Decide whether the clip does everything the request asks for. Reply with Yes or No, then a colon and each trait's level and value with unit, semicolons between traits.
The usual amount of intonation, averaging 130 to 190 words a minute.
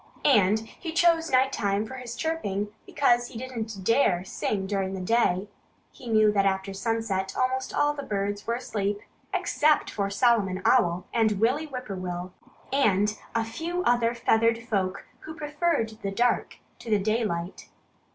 Yes: average, 4.4 semitones; average, 160 wpm